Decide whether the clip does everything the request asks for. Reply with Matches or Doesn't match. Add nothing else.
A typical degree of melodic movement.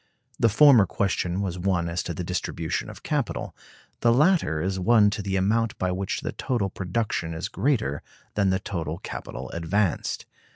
Matches